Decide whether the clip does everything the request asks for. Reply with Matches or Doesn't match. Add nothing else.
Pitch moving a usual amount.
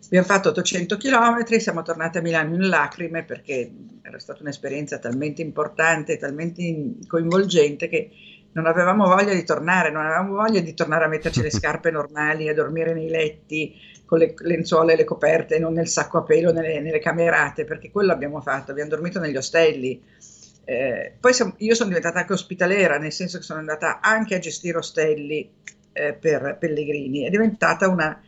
Matches